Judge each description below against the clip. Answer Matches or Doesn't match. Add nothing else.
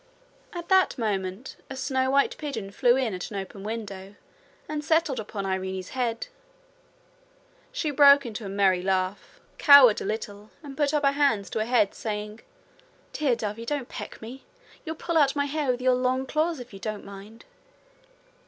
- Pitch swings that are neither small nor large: Doesn't match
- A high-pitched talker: Matches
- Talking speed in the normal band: Matches